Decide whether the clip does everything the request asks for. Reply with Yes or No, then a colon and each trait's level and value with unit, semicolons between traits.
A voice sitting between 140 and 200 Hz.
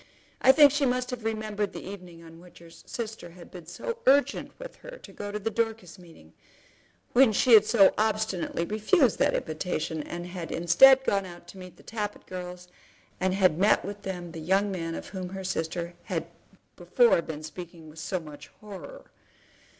Yes: high, 190 Hz